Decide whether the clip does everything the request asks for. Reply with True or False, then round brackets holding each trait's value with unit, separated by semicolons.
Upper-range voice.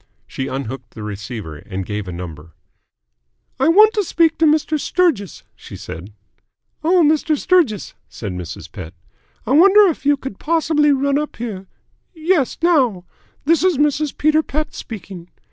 True (275 Hz)